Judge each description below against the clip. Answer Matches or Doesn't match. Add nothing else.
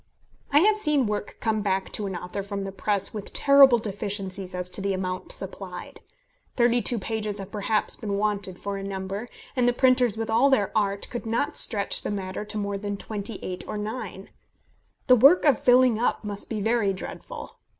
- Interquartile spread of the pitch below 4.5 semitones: Matches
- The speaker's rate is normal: Matches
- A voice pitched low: Doesn't match